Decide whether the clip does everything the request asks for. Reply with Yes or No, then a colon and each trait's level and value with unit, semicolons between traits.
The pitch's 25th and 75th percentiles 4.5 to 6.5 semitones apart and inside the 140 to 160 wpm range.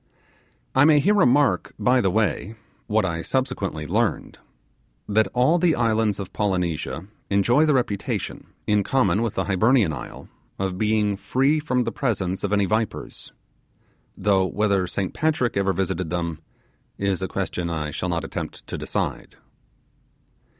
Yes: average, 4.8 semitones; average, 150 wpm